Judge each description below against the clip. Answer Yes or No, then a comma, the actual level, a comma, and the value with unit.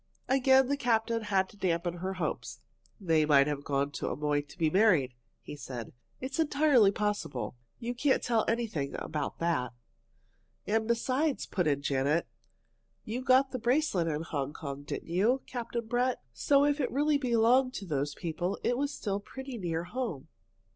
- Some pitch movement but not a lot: No, wide, 8.5 semitones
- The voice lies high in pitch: Yes, high, 205 Hz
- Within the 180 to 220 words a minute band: No, average, 170 wpm